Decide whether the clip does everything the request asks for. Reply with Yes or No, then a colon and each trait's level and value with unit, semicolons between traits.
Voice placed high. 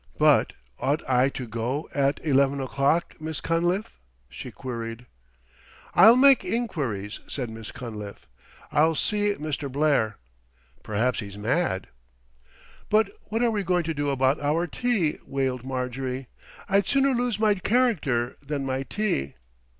No: medium, 140 Hz